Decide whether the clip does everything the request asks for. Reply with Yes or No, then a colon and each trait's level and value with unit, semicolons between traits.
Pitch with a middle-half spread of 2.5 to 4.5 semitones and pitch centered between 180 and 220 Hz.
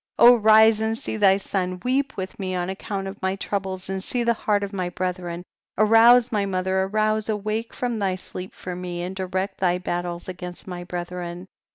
Yes: average, 2.9 semitones; high, 190 Hz